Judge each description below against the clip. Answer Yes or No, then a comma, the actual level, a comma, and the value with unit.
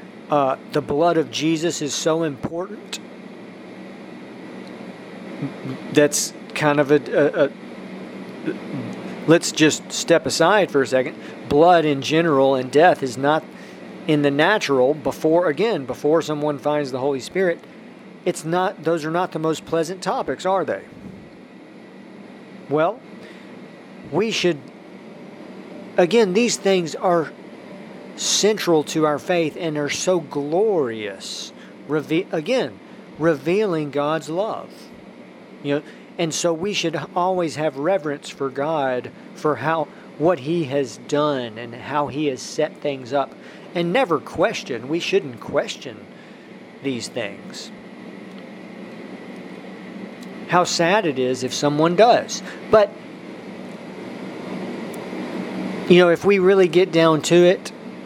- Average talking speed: No, slow, 125 wpm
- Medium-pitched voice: Yes, medium, 160 Hz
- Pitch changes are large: No, average, 3.9 semitones